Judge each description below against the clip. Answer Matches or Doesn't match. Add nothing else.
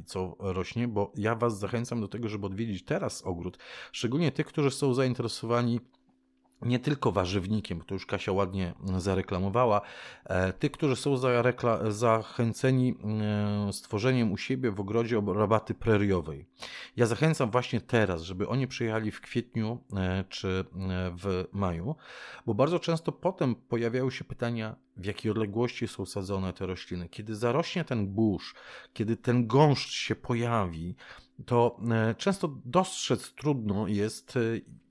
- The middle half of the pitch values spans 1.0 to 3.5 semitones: Doesn't match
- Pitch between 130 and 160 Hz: Doesn't match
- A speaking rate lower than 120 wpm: Doesn't match